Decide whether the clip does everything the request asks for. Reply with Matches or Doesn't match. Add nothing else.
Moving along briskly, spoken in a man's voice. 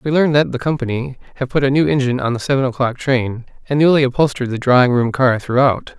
Matches